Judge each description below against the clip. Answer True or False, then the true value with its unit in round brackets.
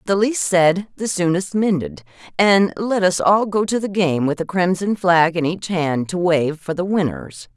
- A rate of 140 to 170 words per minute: False (205 wpm)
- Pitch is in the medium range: True (175 Hz)